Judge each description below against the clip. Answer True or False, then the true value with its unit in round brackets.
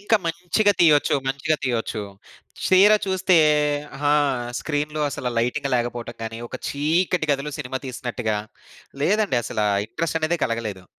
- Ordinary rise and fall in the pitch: False (5.9 semitones)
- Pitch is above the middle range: False (145 Hz)